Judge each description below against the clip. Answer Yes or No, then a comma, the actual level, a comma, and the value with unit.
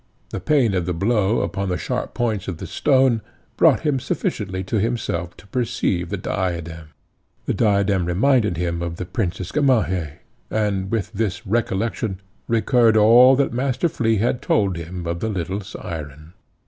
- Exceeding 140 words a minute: Yes, average, 160 wpm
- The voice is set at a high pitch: No, low, 100 Hz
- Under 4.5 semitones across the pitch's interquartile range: No, average, 4.8 semitones